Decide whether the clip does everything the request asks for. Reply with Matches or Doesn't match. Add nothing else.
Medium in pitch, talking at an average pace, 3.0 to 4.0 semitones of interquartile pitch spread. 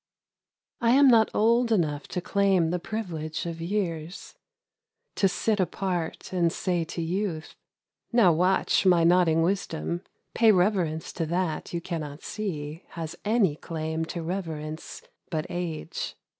Matches